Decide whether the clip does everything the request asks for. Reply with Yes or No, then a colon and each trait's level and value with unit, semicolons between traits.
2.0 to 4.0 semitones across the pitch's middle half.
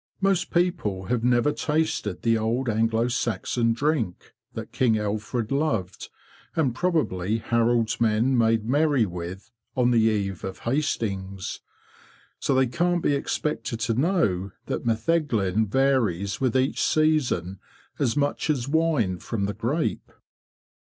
No: average, 5.1 semitones